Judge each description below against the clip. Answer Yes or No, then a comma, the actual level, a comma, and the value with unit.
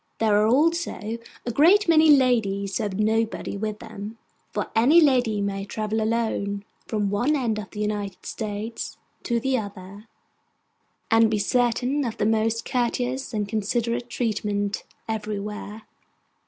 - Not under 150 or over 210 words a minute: No, average, 140 wpm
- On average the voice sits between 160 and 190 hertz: No, high, 220 Hz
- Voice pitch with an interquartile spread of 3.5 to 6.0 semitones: No, average, 2.8 semitones